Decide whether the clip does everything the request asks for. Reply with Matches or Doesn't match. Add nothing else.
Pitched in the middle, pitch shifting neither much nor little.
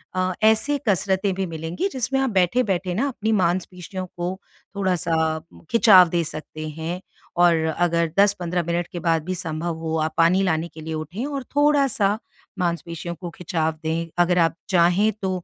Matches